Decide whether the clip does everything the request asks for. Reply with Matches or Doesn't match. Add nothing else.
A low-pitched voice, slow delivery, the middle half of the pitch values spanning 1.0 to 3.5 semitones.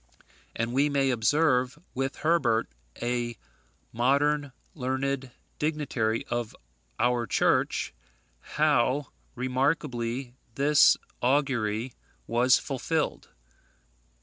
Matches